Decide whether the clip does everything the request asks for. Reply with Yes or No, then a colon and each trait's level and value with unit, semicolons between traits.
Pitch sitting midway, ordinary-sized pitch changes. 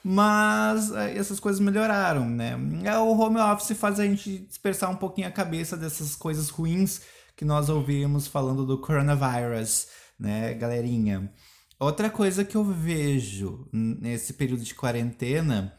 No: medium, 145 Hz; wide, 8.9 semitones